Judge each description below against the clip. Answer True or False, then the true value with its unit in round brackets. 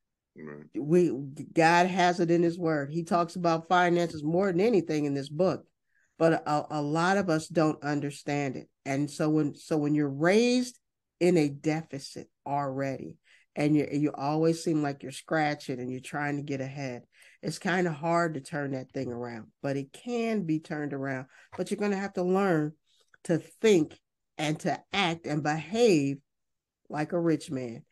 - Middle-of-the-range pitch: True (155 Hz)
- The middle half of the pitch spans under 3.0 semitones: False (3.4 semitones)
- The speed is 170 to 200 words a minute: True (180 wpm)